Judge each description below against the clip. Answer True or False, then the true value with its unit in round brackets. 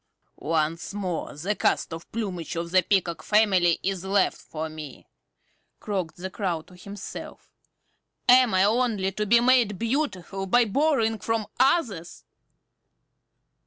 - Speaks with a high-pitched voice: True (195 Hz)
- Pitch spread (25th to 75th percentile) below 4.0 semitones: False (4.5 semitones)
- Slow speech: True (130 wpm)